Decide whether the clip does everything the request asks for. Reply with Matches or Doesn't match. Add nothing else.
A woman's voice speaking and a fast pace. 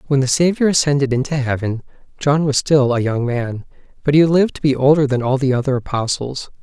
Doesn't match